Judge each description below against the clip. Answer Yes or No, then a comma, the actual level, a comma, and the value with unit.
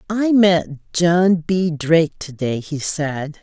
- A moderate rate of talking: Yes, average, 160 wpm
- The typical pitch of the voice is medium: Yes, medium, 165 Hz